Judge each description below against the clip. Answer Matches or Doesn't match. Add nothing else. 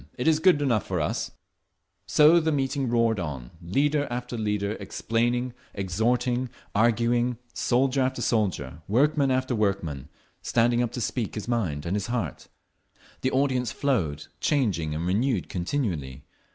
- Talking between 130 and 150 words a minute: Matches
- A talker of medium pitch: Doesn't match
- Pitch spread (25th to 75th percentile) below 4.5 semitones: Doesn't match